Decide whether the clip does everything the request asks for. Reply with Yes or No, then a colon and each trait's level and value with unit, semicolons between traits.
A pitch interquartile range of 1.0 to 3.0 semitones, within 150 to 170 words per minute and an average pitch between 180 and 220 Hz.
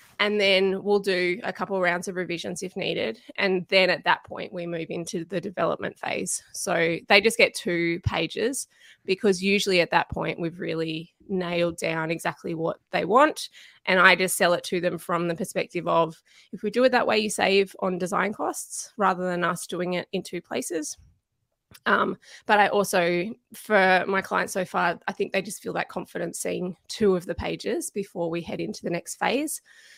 No: average, 2.7 semitones; average, 200 wpm; medium, 185 Hz